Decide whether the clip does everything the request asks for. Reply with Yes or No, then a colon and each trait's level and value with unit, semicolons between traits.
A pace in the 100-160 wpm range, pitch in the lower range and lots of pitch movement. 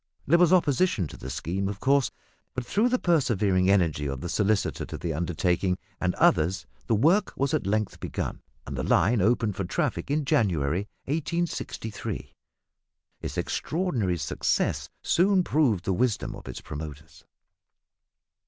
Yes: average, 150 wpm; low, 105 Hz; wide, 8.4 semitones